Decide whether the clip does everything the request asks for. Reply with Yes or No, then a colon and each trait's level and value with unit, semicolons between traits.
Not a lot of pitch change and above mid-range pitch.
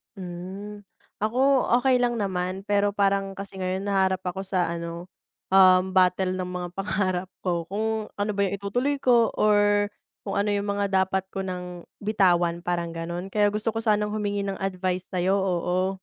Yes: narrow, 2.0 semitones; high, 195 Hz